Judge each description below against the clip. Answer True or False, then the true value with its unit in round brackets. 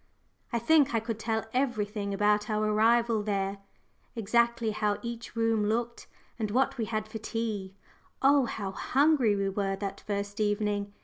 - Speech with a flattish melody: True (2.3 semitones)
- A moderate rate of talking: True (160 wpm)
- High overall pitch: True (215 Hz)